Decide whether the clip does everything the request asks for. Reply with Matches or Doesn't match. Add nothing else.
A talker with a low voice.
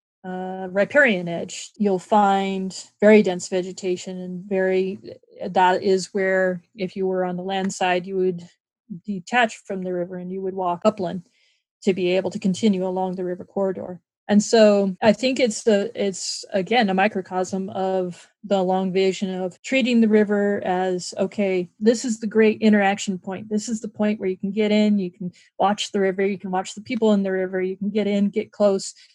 Doesn't match